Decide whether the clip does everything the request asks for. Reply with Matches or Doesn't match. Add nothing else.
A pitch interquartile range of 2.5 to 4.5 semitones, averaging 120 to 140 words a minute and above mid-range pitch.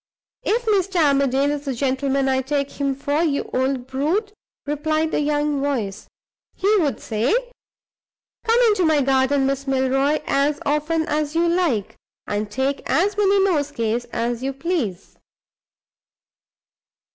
Matches